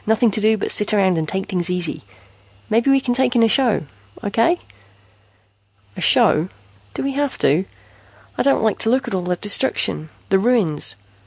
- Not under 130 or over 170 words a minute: No, average, 185 wpm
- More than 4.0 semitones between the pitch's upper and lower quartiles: Yes, average, 5.1 semitones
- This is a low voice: No, high, 215 Hz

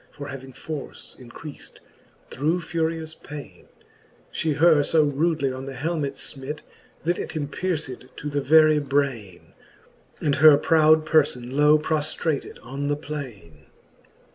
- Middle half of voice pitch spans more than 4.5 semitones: No, average, 2.8 semitones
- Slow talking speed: Yes, slow, 130 wpm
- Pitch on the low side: No, medium, 145 Hz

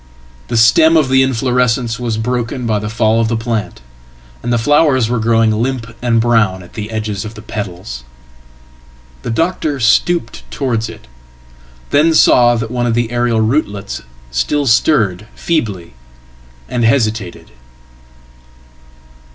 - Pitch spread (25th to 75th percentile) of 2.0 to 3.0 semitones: Yes, average, 2.7 semitones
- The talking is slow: Yes, slow, 125 wpm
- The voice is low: Yes, low, 115 Hz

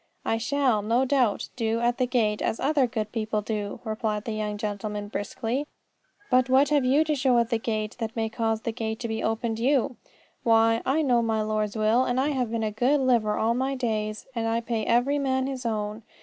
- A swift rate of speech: Yes, fast, 220 wpm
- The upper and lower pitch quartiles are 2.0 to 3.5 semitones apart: Yes, average, 2.9 semitones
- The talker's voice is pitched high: Yes, high, 230 Hz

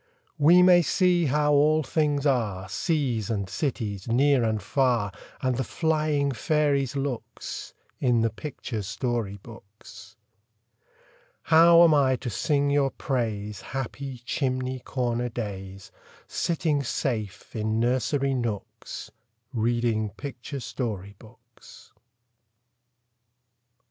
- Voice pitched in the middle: No, low, 125 Hz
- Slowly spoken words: Yes, slow, 110 wpm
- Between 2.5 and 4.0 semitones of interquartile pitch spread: No, average, 4.5 semitones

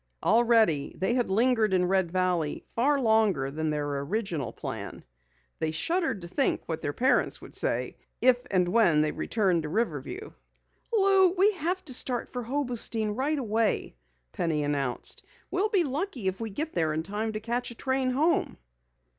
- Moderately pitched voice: No, high, 220 Hz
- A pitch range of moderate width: No, wide, 7.5 semitones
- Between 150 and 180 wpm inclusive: Yes, average, 170 wpm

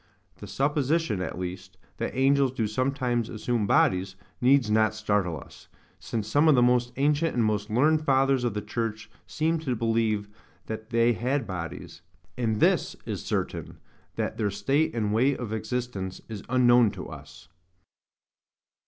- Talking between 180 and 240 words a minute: No, average, 155 wpm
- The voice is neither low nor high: No, low, 115 Hz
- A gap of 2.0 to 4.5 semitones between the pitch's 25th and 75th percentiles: Yes, average, 4.0 semitones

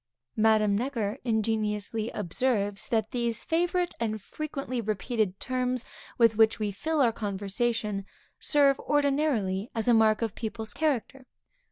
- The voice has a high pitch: Yes, high, 225 Hz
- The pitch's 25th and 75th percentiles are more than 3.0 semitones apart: Yes, average, 3.4 semitones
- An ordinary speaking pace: No, slow, 130 wpm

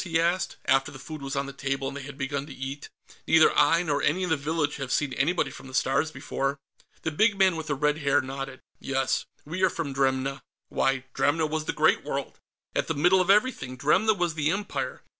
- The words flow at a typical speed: No, fast, 225 wpm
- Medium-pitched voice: Yes, medium, 145 Hz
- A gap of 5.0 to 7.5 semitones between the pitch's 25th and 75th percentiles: No, average, 3.3 semitones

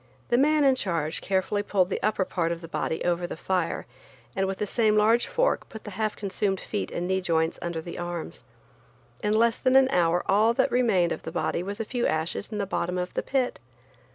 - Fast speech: Yes, fast, 225 wpm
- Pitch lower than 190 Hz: No, high, 195 Hz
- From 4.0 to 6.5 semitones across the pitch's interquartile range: Yes, average, 4.3 semitones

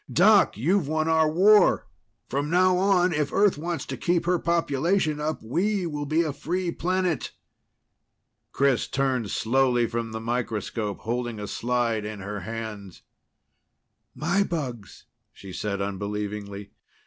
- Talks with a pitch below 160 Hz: Yes, low, 135 Hz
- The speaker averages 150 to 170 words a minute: No, slow, 135 wpm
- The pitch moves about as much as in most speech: No, wide, 7.5 semitones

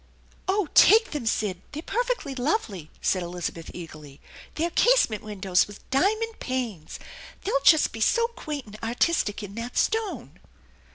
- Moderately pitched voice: No, very high, 250 Hz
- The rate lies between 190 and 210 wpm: No, average, 150 wpm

